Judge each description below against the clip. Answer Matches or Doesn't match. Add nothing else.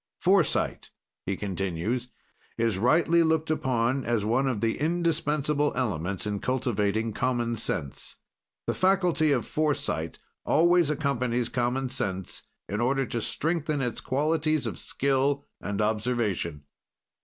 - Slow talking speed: Matches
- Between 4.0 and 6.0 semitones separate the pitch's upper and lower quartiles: Matches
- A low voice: Matches